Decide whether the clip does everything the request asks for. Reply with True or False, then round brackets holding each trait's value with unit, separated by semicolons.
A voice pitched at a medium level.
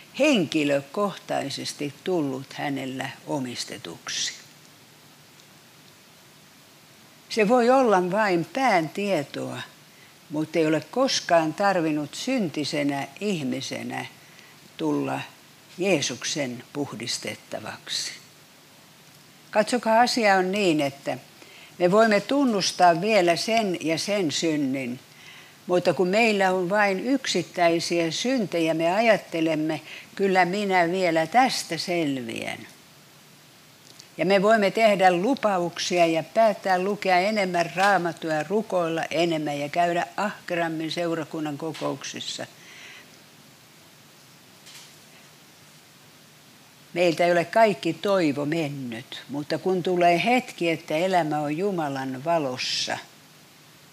True (170 Hz)